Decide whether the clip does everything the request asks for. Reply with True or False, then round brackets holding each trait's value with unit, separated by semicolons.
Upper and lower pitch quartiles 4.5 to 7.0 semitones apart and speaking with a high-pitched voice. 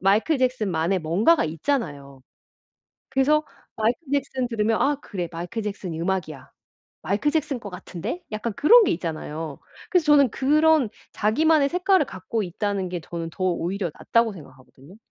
False (8.4 semitones; 210 Hz)